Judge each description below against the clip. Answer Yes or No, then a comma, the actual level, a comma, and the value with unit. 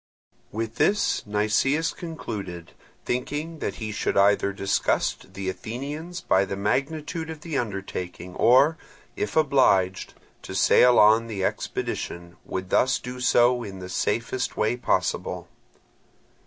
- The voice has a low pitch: Yes, low, 115 Hz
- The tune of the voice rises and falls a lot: Yes, wide, 6.3 semitones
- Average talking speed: No, slow, 130 wpm